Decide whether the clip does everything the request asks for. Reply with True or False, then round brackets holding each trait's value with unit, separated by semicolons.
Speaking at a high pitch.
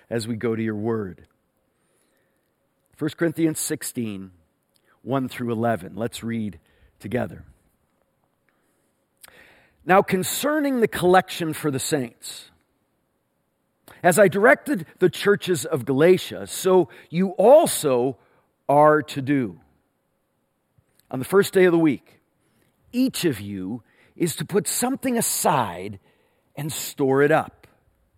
False (140 Hz)